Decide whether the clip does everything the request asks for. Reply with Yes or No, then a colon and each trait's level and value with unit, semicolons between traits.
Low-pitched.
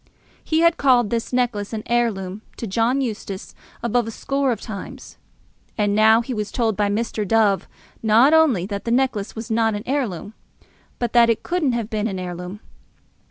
No: high, 225 Hz